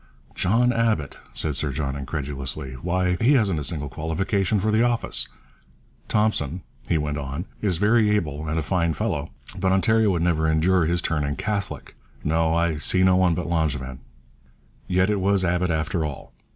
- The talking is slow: No, average, 170 wpm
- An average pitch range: Yes, average, 4.4 semitones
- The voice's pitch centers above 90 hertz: No, very low, 85 Hz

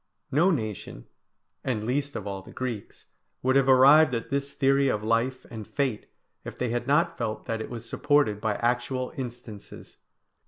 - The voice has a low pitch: Yes, low, 125 Hz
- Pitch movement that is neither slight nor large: Yes, average, 3.6 semitones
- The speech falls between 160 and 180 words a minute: Yes, average, 170 wpm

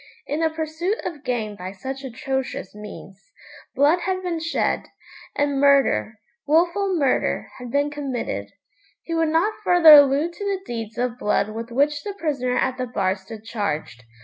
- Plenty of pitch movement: Yes, wide, 6.0 semitones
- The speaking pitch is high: Yes, very high, 275 Hz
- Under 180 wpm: Yes, average, 165 wpm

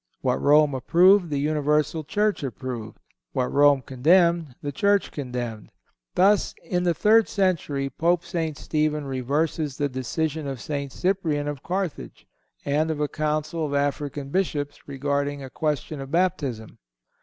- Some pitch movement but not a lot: Yes, average, 3.4 semitones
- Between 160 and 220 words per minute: No, average, 145 wpm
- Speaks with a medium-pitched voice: Yes, medium, 150 Hz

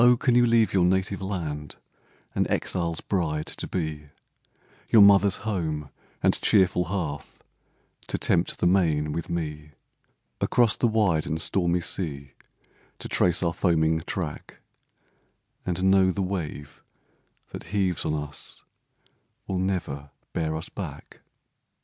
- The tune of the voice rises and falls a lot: No, average, 3.8 semitones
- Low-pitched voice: Yes, very low, 85 Hz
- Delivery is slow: Yes, slow, 130 wpm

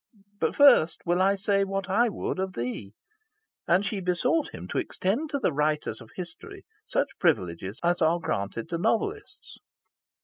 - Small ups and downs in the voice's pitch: No, average, 4.9 semitones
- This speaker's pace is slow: No, average, 165 wpm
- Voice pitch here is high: No, medium, 180 Hz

